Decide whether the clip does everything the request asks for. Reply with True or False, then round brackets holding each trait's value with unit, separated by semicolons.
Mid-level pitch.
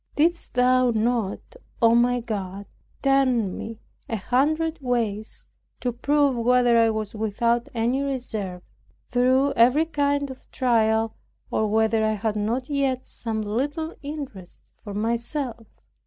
False (240 Hz)